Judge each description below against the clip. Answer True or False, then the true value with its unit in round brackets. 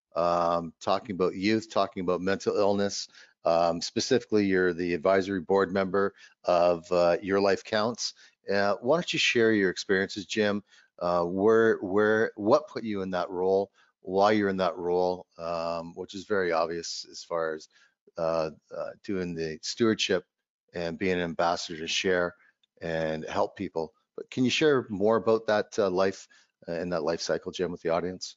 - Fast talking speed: False (170 wpm)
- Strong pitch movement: False (2.8 semitones)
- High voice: False (95 Hz)